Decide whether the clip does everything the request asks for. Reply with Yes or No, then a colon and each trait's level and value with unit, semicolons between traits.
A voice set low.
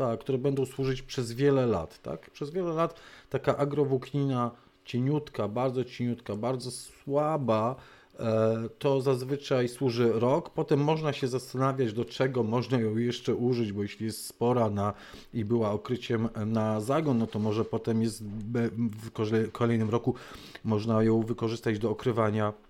Yes: low, 120 Hz